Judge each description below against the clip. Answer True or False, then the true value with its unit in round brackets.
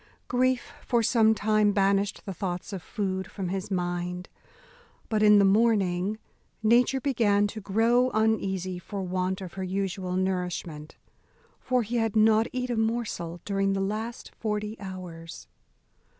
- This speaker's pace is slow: False (145 wpm)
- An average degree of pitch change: True (3.0 semitones)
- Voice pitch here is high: True (200 Hz)